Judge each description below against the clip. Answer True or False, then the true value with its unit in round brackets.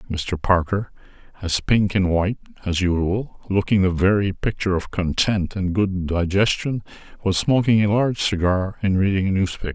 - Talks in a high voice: False (95 Hz)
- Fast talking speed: False (160 wpm)